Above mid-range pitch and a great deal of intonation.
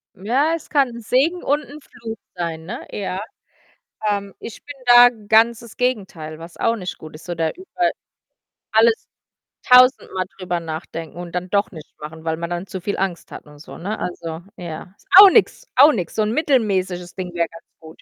Yes: high, 195 Hz; wide, 6.1 semitones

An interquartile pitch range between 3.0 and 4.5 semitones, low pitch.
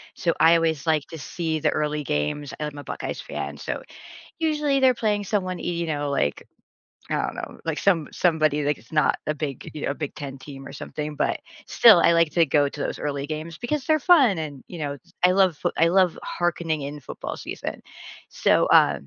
No: average, 3.6 semitones; medium, 155 Hz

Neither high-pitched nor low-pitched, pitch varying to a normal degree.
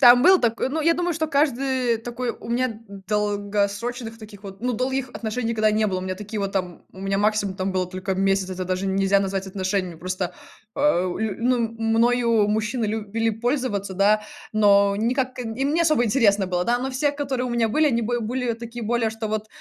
No: high, 220 Hz; average, 3.7 semitones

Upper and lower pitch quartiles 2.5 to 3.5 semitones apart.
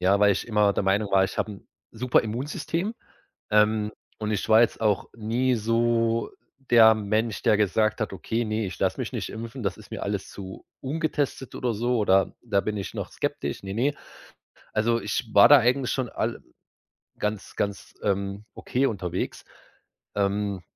Yes: average, 2.8 semitones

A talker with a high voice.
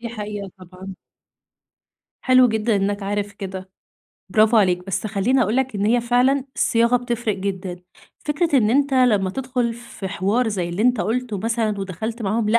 Yes: high, 220 Hz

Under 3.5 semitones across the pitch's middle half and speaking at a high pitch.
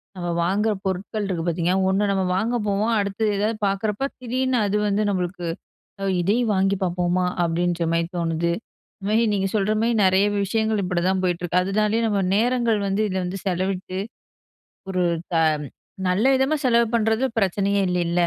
Yes: average, 3.1 semitones; high, 195 Hz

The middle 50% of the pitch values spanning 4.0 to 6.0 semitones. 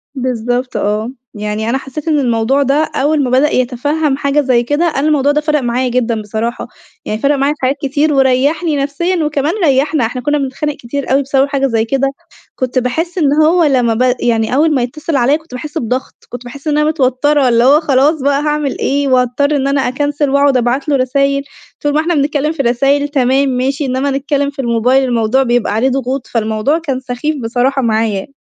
No: average, 2.8 semitones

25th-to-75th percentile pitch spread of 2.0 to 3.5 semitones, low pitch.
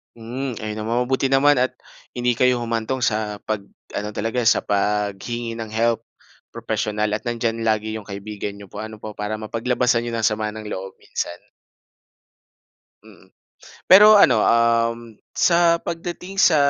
Yes: narrow, 2.6 semitones; low, 115 Hz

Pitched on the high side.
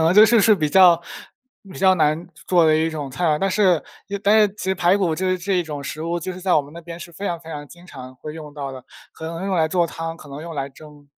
No: medium, 165 Hz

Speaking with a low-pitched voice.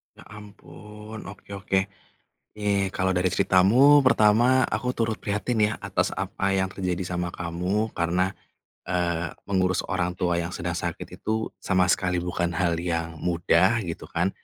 Yes: very low, 95 Hz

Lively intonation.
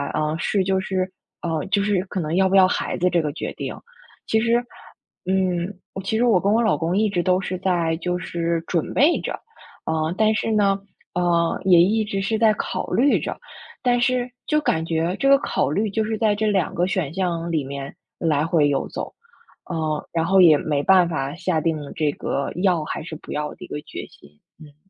No: average, 4.1 semitones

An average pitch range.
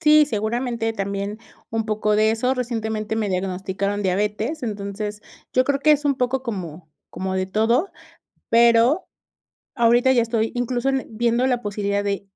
Yes: average, 3.4 semitones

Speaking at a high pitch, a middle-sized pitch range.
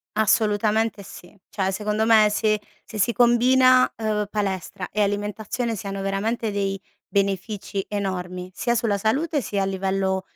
No: high, 210 Hz; narrow, 2.3 semitones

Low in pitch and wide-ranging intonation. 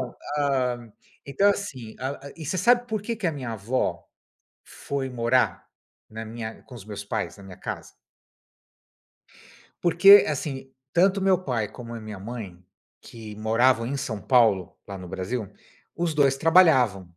Yes: low, 125 Hz; wide, 6.2 semitones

